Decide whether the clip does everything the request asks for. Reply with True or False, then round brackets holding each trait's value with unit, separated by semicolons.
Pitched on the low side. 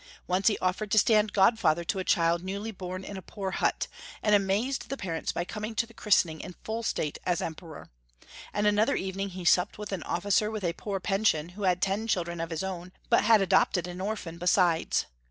False (190 Hz)